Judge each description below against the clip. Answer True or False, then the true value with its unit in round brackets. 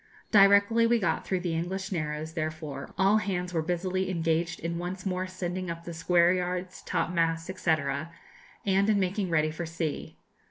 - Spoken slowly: False (170 wpm)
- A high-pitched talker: False (180 Hz)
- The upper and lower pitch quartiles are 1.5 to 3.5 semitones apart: True (2.5 semitones)